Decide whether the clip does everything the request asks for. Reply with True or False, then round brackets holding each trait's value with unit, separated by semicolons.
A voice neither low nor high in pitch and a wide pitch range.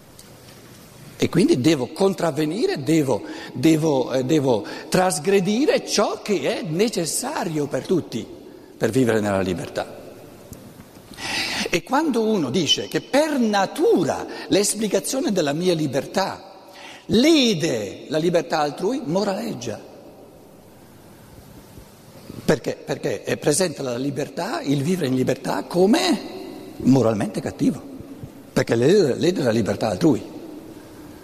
True (175 Hz; 7.3 semitones)